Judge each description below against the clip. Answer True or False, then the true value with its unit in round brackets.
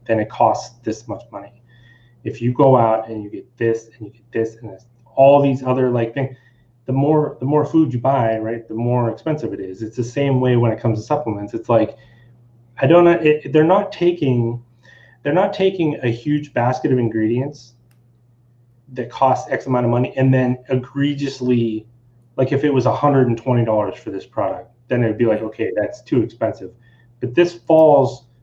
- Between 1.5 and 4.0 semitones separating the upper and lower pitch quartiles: True (3.0 semitones)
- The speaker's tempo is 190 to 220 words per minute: True (195 wpm)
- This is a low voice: True (120 Hz)